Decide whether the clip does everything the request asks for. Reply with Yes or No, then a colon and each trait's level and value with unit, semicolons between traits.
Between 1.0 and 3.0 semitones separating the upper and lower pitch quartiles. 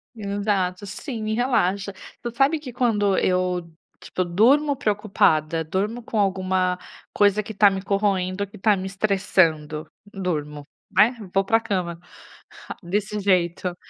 Yes: average, 2.7 semitones